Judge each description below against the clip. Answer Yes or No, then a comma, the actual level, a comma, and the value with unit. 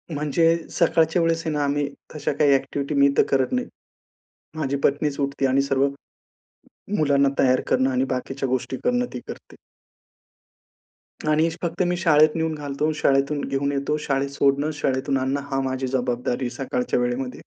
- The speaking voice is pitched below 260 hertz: Yes, medium, 140 Hz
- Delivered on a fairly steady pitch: Yes, narrow, 2.3 semitones